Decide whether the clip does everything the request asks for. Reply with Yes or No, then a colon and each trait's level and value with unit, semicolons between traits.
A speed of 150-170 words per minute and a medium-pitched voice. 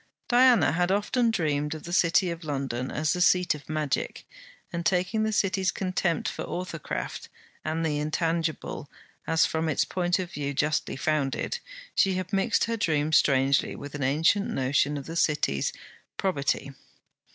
Yes: average, 160 wpm; medium, 160 Hz